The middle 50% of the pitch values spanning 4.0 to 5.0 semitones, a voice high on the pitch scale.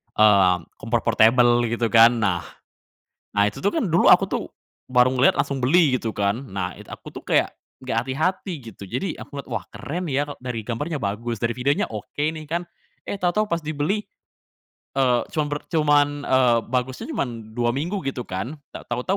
No: average, 4.6 semitones; low, 125 Hz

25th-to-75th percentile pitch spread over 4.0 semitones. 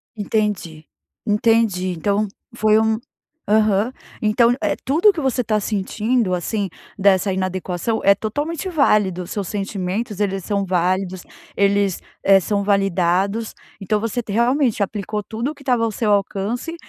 No: average, 2.9 semitones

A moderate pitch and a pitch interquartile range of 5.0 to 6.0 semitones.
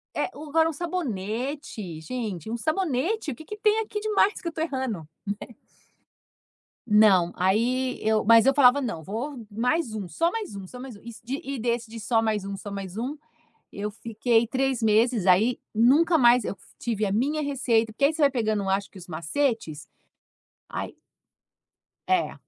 No: high, 235 Hz; average, 5.3 semitones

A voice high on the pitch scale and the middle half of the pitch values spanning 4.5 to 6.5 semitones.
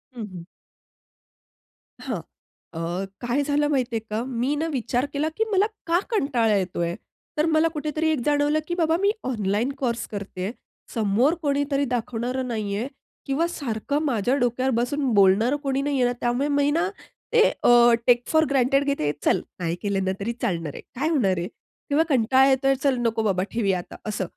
Yes: very high, 250 Hz; average, 5.0 semitones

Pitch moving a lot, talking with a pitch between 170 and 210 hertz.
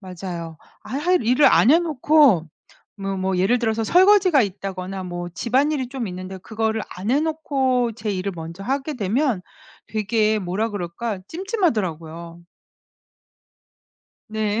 No: wide, 6.4 semitones; high, 220 Hz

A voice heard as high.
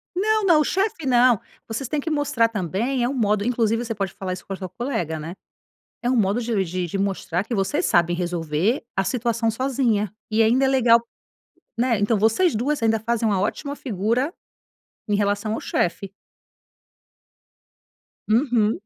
Yes: high, 225 Hz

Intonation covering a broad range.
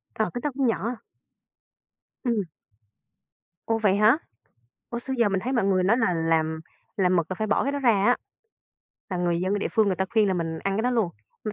No: average, 4.2 semitones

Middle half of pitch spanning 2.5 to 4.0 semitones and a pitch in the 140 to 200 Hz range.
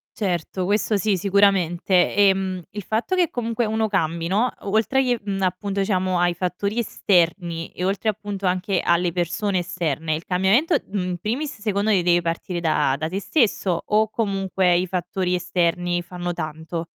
Yes: average, 2.9 semitones; medium, 185 Hz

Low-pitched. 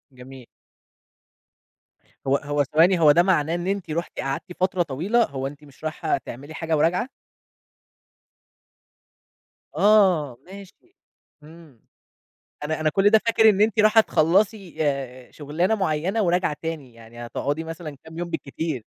No: medium, 160 Hz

